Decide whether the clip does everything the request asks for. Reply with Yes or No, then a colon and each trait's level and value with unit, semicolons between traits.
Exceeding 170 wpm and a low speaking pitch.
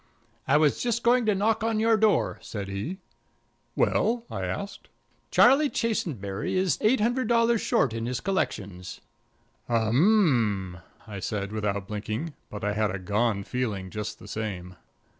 No: average, 155 wpm; low, 120 Hz